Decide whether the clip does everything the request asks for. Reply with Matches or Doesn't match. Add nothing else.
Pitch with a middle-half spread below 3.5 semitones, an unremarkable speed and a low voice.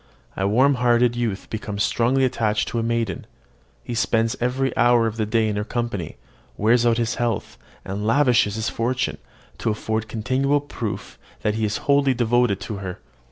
Matches